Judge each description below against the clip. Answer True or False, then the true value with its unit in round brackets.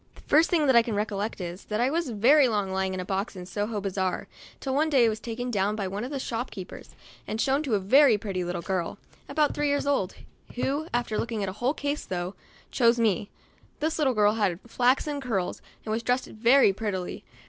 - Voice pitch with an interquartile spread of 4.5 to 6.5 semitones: True (5.2 semitones)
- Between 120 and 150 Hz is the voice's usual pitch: False (225 Hz)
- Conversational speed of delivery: False (215 wpm)